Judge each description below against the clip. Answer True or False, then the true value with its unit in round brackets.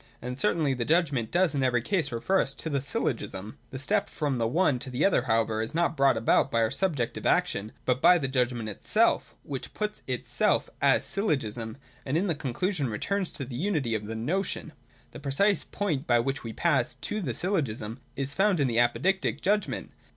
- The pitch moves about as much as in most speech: False (6.5 semitones)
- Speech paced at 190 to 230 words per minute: True (200 wpm)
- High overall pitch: False (135 Hz)